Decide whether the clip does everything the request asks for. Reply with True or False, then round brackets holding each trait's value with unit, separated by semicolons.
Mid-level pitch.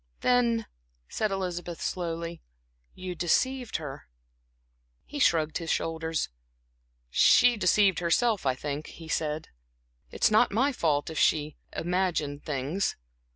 True (170 Hz)